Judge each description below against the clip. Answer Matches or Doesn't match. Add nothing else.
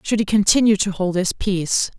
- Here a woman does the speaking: Matches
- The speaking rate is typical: Doesn't match